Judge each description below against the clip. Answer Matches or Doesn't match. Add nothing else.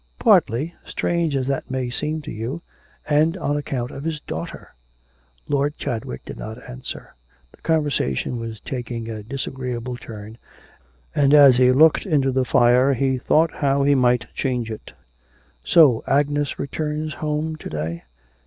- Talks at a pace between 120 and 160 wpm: Matches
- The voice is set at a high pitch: Doesn't match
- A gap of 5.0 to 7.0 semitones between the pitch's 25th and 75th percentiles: Doesn't match